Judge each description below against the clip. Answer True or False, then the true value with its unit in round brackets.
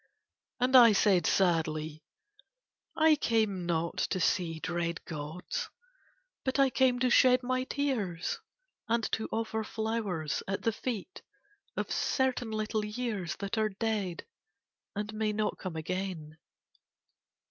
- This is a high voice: True (215 Hz)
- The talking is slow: True (125 wpm)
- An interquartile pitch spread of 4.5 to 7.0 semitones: True (5.5 semitones)